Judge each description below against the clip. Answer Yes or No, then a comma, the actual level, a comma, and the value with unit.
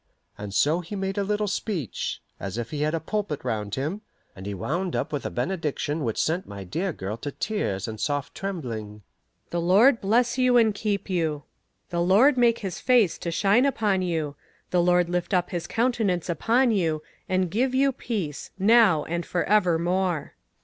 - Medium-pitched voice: Yes, medium, 180 Hz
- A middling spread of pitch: No, wide, 5.8 semitones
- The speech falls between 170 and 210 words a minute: Yes, average, 185 wpm